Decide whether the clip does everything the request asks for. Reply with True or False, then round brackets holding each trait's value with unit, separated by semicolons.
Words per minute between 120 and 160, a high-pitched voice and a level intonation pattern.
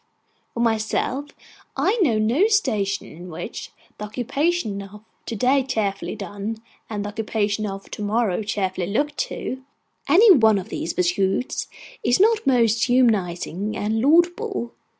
False (140 wpm; 220 Hz; 4.8 semitones)